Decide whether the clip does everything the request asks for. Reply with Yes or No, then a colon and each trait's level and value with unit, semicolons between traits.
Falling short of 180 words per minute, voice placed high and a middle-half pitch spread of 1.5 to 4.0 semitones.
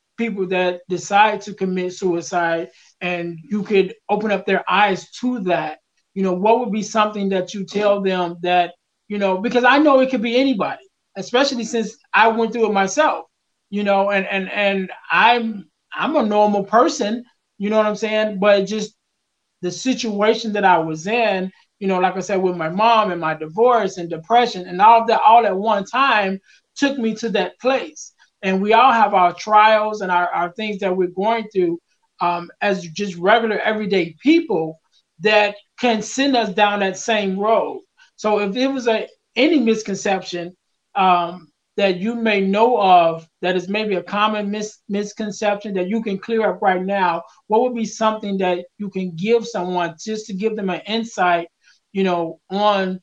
No: average, 185 wpm; high, 205 Hz; average, 3.3 semitones